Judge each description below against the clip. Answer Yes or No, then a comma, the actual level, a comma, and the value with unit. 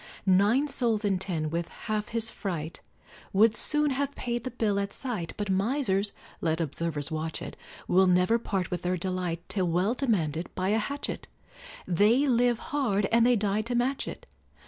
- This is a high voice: Yes, high, 205 Hz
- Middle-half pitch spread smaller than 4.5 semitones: No, average, 4.8 semitones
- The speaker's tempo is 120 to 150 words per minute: No, average, 175 wpm